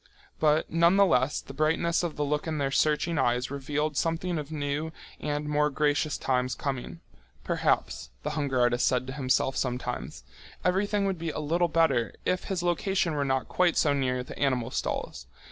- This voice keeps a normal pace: Yes, average, 175 wpm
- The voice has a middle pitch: Yes, medium, 150 Hz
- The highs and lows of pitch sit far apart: No, average, 3.8 semitones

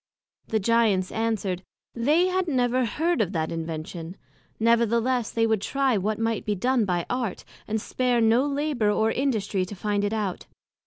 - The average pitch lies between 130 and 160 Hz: No, high, 225 Hz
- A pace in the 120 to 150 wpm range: No, average, 165 wpm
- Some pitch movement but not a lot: Yes, average, 3.7 semitones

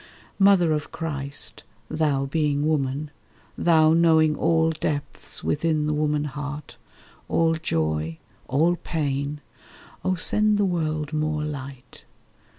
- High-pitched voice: No, medium, 150 Hz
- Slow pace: Yes, slow, 115 wpm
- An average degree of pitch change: No, narrow, 2.1 semitones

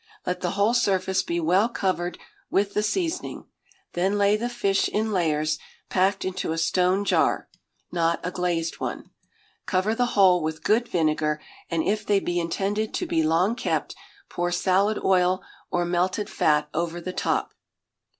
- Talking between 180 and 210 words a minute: No, average, 160 wpm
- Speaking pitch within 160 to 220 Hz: Yes, medium, 185 Hz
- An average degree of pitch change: Yes, average, 3.0 semitones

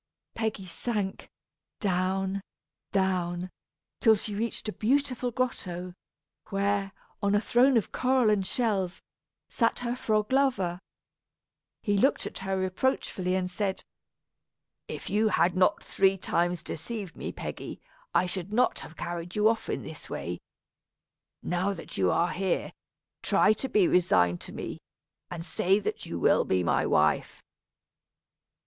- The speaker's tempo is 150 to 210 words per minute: No, average, 140 wpm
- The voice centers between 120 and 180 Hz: No, high, 195 Hz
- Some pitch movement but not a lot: Yes, average, 3.5 semitones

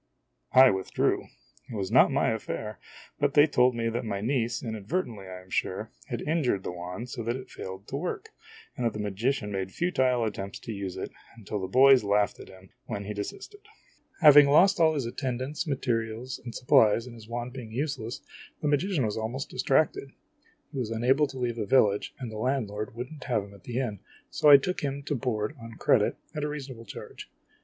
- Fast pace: Yes, fast, 215 wpm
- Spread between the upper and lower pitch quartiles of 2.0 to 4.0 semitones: No, average, 4.4 semitones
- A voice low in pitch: Yes, low, 120 Hz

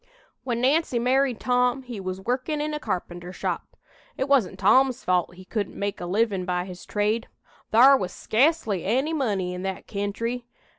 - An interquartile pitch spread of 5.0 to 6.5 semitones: Yes, wide, 5.6 semitones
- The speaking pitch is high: Yes, high, 225 Hz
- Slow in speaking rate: No, average, 175 wpm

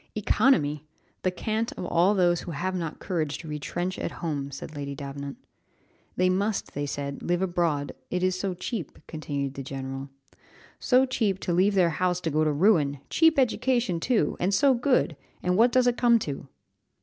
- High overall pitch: No, medium, 175 Hz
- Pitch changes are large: Yes, wide, 6.2 semitones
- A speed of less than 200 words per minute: Yes, average, 185 wpm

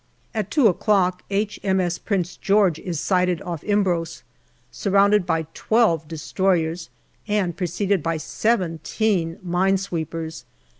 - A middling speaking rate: No, slow, 110 wpm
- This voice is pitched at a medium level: Yes, medium, 180 Hz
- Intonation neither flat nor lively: Yes, average, 3.3 semitones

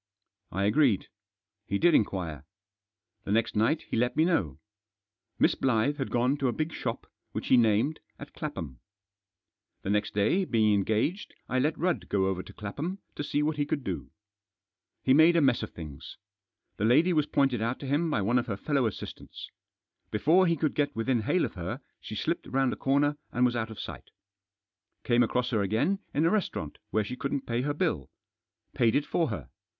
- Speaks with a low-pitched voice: Yes, low, 125 Hz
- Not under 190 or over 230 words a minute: Yes, average, 195 wpm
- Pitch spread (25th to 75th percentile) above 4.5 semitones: Yes, wide, 5.6 semitones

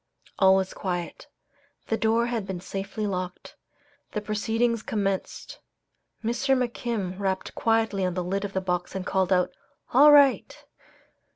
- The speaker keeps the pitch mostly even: No, average, 3.2 semitones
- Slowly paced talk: No, average, 145 wpm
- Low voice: No, high, 200 Hz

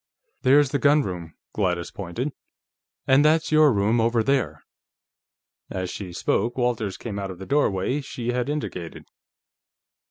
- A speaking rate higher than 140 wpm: No, slow, 135 wpm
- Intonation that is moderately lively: No, wide, 6.5 semitones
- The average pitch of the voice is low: Yes, low, 120 Hz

